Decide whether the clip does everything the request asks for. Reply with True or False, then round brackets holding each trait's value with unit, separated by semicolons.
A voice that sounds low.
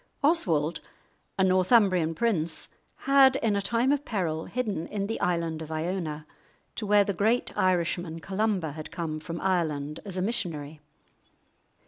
False (185 Hz)